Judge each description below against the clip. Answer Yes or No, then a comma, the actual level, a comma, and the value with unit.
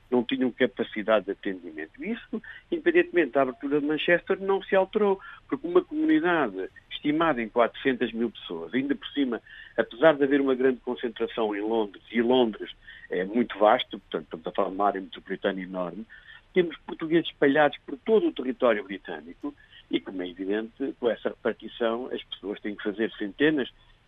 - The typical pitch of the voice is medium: No, low, 130 Hz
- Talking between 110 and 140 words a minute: No, average, 170 wpm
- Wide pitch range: Yes, wide, 8.9 semitones